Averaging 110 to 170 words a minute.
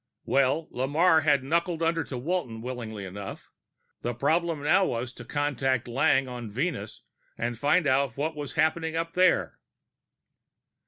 Yes: average, 145 wpm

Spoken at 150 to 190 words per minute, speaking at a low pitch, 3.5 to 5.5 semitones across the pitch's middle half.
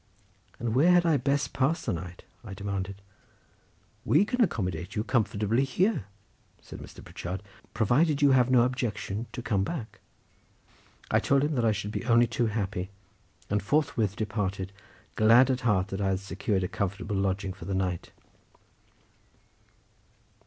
Yes: average, 155 wpm; low, 110 Hz; average, 4.8 semitones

